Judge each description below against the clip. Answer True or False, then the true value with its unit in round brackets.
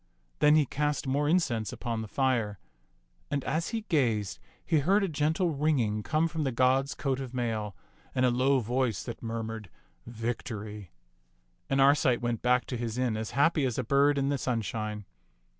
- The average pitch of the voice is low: True (130 Hz)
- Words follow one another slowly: False (175 wpm)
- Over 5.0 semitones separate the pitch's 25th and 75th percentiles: False (4.2 semitones)